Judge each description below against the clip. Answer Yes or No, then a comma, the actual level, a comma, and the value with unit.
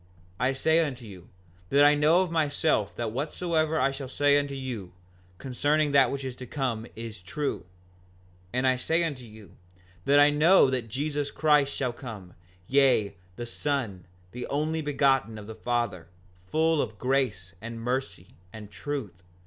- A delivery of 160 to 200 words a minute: Yes, average, 165 wpm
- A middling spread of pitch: Yes, average, 4.2 semitones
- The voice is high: No, low, 135 Hz